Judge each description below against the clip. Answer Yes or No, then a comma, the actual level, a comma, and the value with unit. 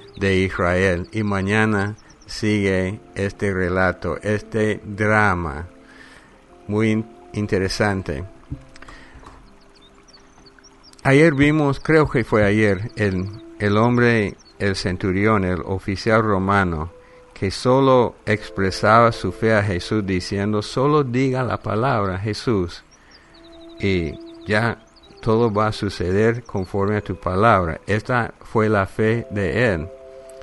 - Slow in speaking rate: Yes, slow, 105 wpm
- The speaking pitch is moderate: No, low, 105 Hz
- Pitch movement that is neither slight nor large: Yes, average, 3.1 semitones